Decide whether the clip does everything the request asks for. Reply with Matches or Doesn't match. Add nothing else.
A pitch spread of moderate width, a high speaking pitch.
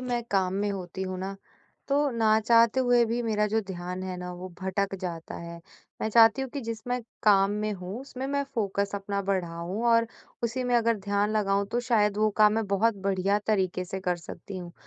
Matches